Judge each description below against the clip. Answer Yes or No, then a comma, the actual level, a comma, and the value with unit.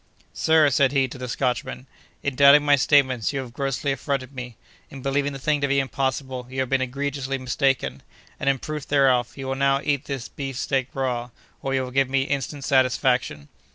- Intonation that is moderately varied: No, narrow, 1.5 semitones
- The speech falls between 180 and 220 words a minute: Yes, average, 200 wpm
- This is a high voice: No, low, 135 Hz